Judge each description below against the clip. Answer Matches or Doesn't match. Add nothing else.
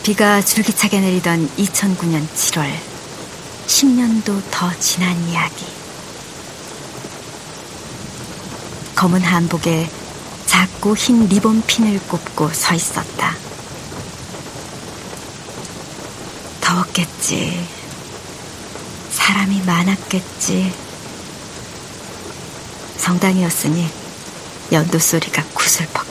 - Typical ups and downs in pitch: Matches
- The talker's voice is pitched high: Doesn't match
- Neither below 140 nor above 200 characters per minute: Matches